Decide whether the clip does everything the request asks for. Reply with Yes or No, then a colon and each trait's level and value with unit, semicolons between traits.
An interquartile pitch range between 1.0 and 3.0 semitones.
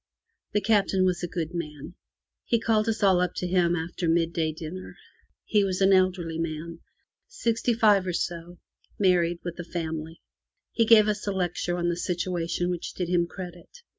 Yes: narrow, 2.5 semitones